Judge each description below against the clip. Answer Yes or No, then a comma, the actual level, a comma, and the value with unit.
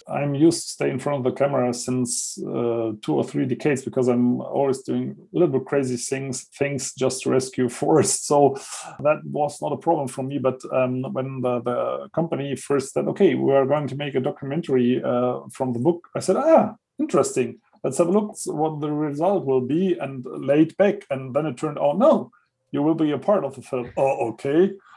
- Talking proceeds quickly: Yes, fast, 215 wpm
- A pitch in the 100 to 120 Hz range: No, medium, 140 Hz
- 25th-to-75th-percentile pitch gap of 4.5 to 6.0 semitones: No, average, 3.1 semitones